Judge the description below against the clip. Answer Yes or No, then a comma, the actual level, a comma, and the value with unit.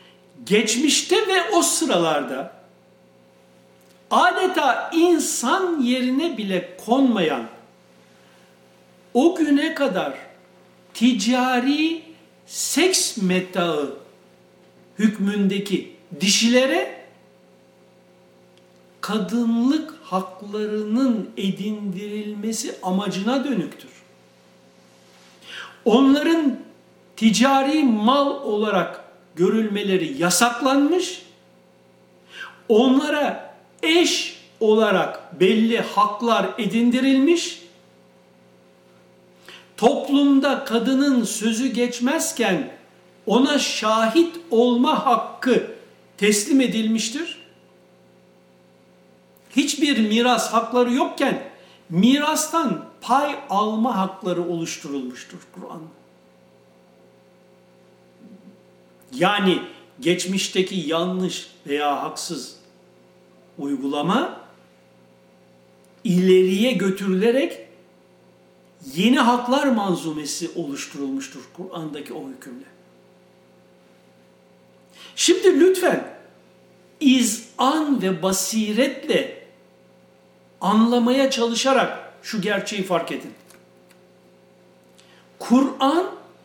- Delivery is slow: Yes, slow, 55 wpm